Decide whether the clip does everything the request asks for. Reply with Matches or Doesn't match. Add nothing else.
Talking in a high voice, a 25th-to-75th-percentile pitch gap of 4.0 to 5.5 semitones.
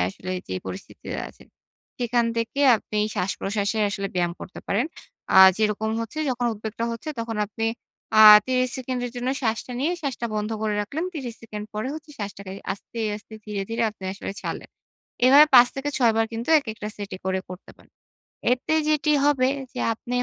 Doesn't match